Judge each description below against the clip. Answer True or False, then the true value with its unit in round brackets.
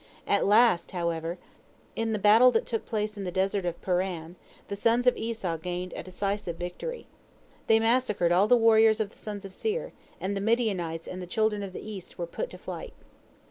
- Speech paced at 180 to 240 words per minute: True (200 wpm)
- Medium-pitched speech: False (200 Hz)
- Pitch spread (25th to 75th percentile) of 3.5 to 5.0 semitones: True (3.9 semitones)